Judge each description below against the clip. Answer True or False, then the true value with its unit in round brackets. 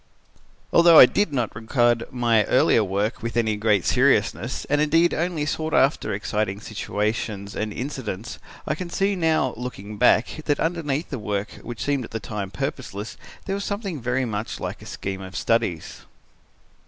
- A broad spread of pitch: True (6.0 semitones)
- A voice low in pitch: True (120 Hz)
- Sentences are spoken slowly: False (165 wpm)